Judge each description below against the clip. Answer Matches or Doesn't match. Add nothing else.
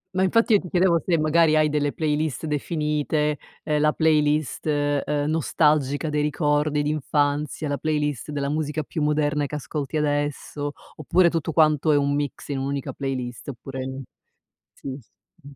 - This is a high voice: Doesn't match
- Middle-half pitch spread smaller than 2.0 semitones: Matches